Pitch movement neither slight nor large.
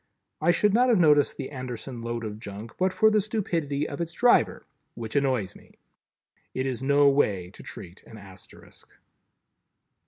No: wide, 7.2 semitones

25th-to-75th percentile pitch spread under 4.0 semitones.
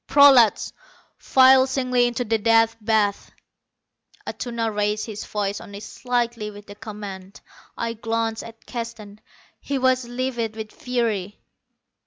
Yes: narrow, 2.6 semitones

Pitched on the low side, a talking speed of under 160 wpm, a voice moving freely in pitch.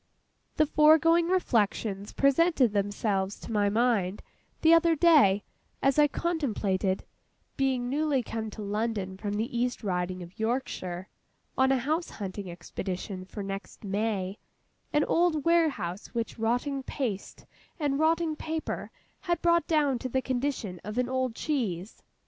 No: high, 240 Hz; average, 140 wpm; wide, 6.9 semitones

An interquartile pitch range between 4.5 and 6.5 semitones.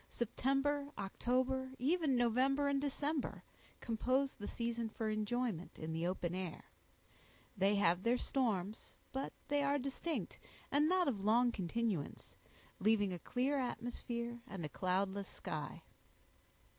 Yes: average, 5.2 semitones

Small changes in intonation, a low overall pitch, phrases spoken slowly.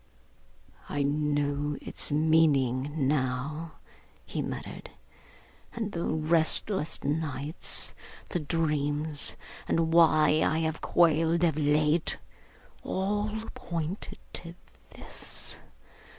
No: narrow, 2.2 semitones; medium, 155 Hz; slow, 90 wpm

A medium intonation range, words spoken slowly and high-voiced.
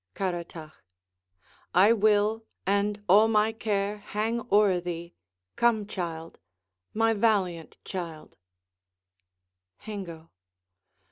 Yes: average, 3.6 semitones; slow, 80 wpm; high, 205 Hz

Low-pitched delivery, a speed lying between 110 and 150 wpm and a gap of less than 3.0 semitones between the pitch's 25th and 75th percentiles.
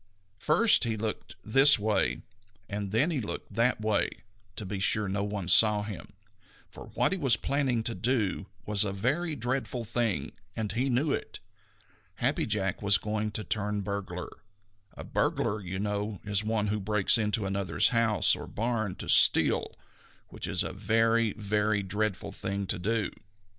No: low, 105 Hz; average, 170 wpm; narrow, 2.4 semitones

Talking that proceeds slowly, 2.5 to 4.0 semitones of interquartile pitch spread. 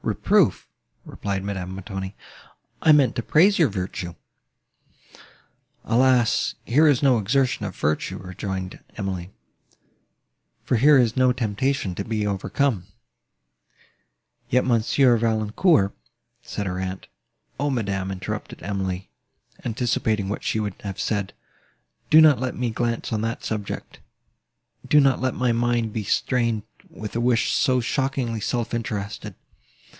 No: slow, 130 wpm; average, 4.4 semitones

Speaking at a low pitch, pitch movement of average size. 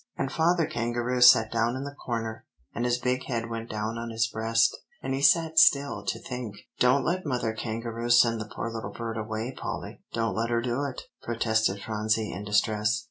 No: low, 115 Hz; narrow, 2.1 semitones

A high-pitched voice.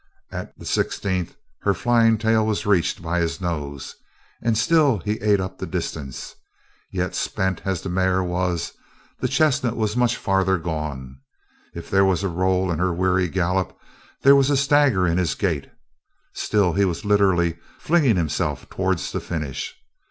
No: very low, 95 Hz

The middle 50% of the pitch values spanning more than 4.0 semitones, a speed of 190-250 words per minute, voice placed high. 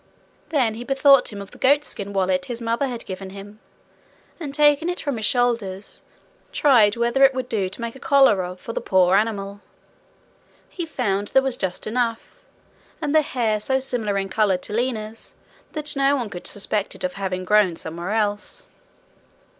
No: average, 5.2 semitones; average, 180 wpm; high, 225 Hz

